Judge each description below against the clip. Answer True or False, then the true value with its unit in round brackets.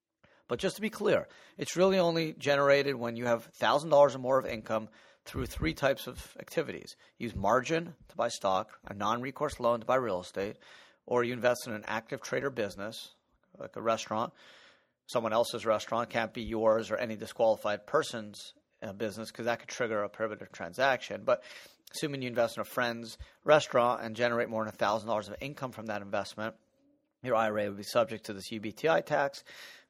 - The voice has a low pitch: True (120 Hz)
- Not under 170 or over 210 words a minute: True (180 wpm)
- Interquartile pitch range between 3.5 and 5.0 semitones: True (4.1 semitones)